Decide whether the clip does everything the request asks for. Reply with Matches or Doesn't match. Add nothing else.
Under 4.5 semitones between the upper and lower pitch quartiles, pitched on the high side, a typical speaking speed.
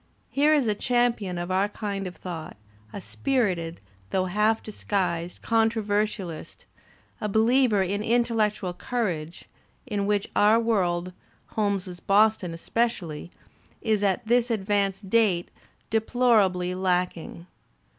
Doesn't match